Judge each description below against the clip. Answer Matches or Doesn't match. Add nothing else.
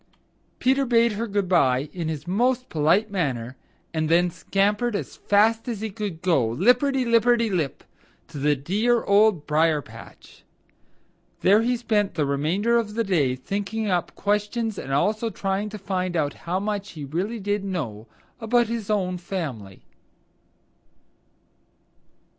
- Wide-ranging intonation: Matches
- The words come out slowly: Doesn't match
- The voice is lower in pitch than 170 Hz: Doesn't match